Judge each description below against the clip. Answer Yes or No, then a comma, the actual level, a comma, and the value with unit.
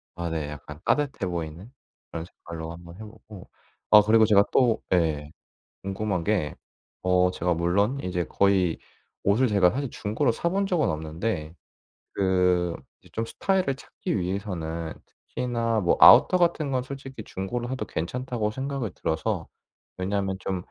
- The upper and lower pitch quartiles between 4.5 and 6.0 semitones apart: Yes, average, 5.3 semitones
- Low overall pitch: Yes, low, 100 Hz